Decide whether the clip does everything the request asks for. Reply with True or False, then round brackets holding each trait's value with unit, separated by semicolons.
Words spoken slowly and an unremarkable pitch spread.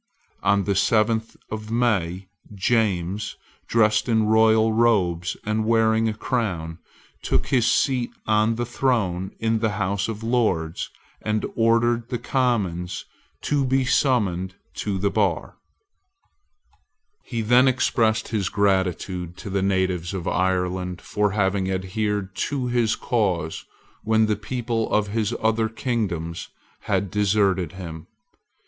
True (130 wpm; 3.4 semitones)